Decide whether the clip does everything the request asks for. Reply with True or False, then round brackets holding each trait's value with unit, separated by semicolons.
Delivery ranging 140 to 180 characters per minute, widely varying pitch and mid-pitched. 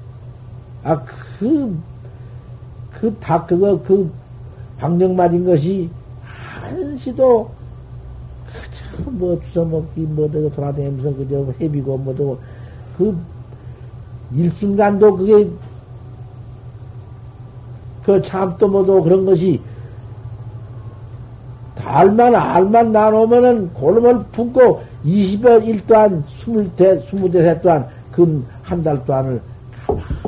True (170 characters per minute; 7.8 semitones; 145 Hz)